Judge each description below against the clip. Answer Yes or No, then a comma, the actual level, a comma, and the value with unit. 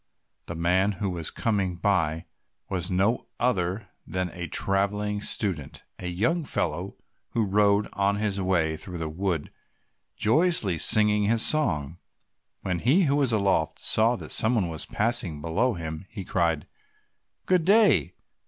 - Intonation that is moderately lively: Yes, average, 4.1 semitones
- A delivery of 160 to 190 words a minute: No, average, 145 wpm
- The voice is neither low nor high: No, low, 100 Hz